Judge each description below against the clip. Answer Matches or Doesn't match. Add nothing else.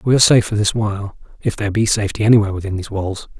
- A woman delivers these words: Doesn't match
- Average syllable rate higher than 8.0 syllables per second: Matches